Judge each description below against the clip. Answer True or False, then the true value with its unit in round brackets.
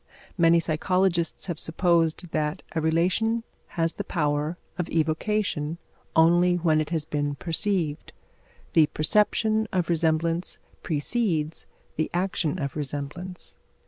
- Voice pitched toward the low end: False (165 Hz)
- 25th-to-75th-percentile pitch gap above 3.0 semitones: False (2.6 semitones)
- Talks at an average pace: False (115 wpm)